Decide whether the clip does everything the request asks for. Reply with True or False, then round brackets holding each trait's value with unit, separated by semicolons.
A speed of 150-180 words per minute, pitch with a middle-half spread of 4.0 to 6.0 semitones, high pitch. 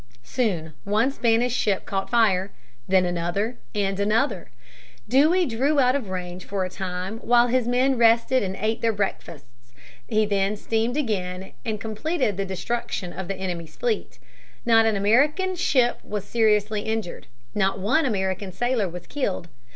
True (160 wpm; 4.3 semitones; 215 Hz)